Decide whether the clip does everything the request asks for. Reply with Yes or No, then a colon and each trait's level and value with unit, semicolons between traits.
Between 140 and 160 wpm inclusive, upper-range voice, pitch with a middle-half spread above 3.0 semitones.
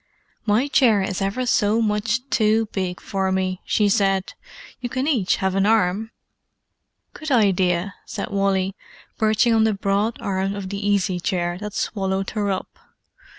No: average, 155 wpm; high, 200 Hz; narrow, 2.5 semitones